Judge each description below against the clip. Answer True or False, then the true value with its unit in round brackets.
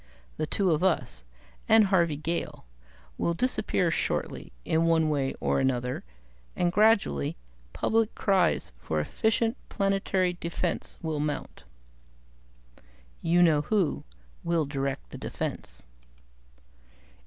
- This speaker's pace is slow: True (110 wpm)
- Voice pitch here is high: False (170 Hz)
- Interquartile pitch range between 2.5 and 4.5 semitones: False (4.9 semitones)